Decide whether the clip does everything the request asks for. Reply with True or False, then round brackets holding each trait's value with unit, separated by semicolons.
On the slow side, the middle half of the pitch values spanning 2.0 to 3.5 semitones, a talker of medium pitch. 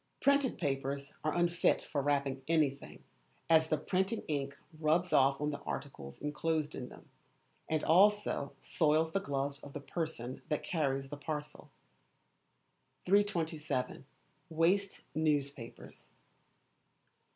True (120 wpm; 3.0 semitones; 150 Hz)